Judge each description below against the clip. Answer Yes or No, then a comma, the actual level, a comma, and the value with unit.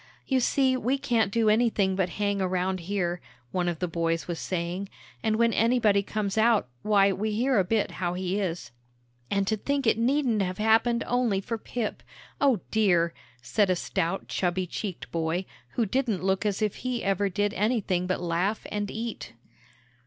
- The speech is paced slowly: No, average, 180 wpm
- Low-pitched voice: No, high, 200 Hz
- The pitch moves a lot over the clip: No, average, 3.6 semitones